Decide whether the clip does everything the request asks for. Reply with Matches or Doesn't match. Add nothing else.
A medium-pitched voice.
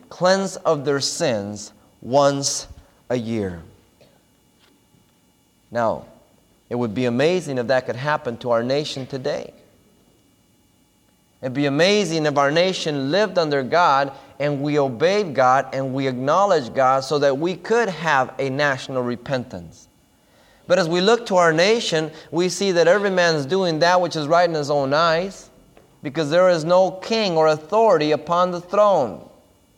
Matches